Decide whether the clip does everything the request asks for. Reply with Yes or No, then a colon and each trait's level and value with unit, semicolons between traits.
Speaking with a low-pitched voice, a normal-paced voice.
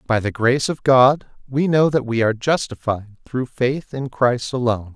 Yes: low, 125 Hz; average, 195 wpm